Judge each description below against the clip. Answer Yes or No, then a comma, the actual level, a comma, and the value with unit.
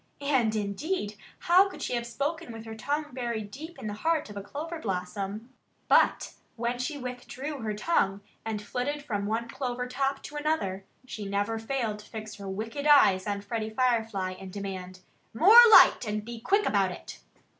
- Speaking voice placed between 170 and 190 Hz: No, high, 225 Hz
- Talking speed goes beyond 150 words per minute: Yes, average, 180 wpm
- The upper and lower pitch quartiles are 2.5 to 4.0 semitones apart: No, wide, 5.5 semitones